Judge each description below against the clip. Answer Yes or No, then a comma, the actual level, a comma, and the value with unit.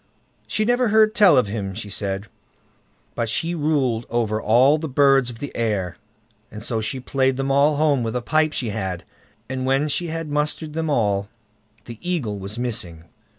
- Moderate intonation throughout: No, wide, 5.8 semitones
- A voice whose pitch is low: Yes, low, 130 Hz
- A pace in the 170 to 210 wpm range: Yes, average, 185 wpm